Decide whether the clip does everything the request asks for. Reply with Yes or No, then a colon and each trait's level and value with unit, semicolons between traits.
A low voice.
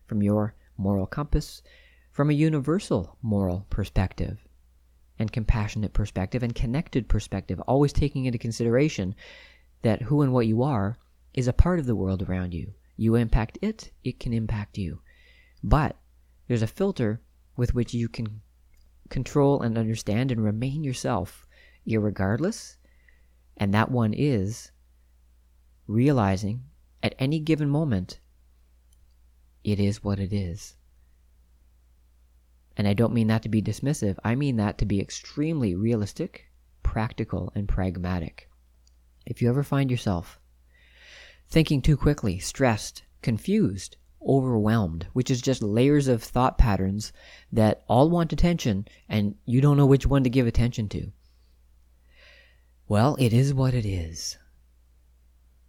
Yes: low, 105 Hz